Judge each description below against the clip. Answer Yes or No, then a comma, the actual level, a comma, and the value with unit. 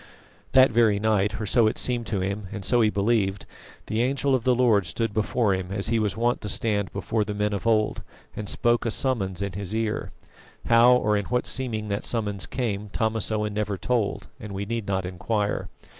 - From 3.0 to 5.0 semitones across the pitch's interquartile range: No, narrow, 2.5 semitones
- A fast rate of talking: Yes, fast, 210 wpm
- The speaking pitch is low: Yes, low, 105 Hz